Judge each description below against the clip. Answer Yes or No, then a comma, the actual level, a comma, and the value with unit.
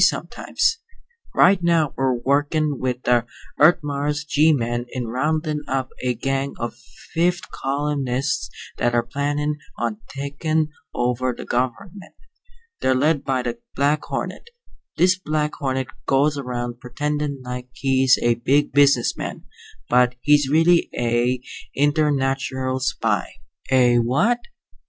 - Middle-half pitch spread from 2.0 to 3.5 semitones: Yes, average, 3.2 semitones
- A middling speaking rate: No, slow, 130 wpm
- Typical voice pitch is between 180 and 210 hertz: No, low, 135 Hz